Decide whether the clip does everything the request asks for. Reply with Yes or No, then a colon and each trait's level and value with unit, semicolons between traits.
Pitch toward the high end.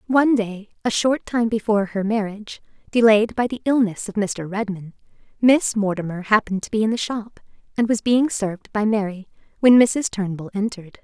Yes: high, 215 Hz